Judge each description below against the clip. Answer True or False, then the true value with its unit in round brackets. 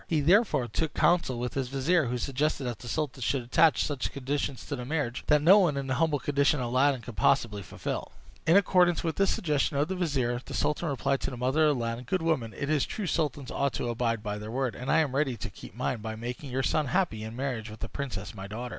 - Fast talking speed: True (250 wpm)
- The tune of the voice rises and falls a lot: False (4.1 semitones)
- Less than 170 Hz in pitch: True (135 Hz)